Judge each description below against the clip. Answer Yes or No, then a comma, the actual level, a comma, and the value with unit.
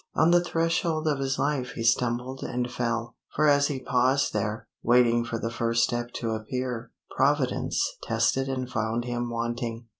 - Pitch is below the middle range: Yes, low, 125 Hz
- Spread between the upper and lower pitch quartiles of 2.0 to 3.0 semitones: Yes, narrow, 2.4 semitones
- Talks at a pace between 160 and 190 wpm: Yes, average, 170 wpm